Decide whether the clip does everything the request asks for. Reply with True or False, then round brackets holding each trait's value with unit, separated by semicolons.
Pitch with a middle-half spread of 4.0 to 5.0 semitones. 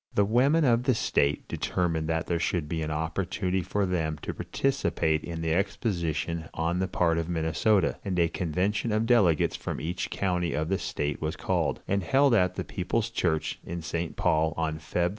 False (3.6 semitones)